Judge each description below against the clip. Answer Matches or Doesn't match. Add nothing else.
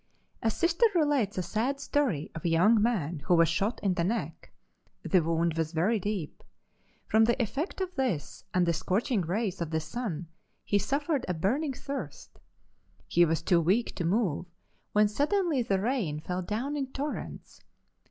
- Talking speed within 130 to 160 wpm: Doesn't match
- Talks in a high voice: Matches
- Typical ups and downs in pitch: Doesn't match